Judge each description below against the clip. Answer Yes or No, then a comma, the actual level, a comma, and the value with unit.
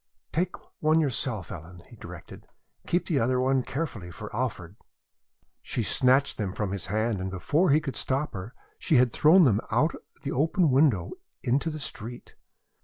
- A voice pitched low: Yes, low, 125 Hz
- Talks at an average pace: Yes, average, 175 wpm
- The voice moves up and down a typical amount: No, wide, 6.6 semitones